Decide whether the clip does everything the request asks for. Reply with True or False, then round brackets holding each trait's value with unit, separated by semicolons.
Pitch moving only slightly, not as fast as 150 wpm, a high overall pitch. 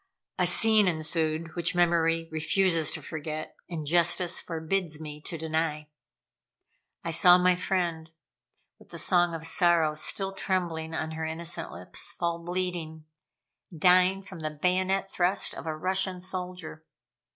False (2.3 semitones; 140 wpm; 170 Hz)